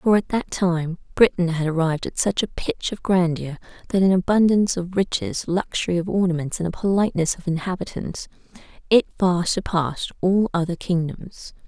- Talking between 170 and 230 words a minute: No, average, 160 wpm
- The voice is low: No, medium, 180 Hz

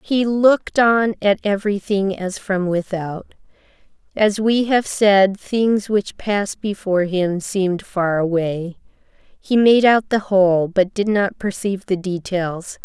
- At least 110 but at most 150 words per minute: Yes, average, 145 wpm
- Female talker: Yes, female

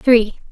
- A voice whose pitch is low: No, high, 230 Hz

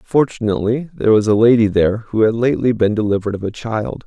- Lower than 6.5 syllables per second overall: No, 6.6 syllables/s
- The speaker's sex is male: Yes, male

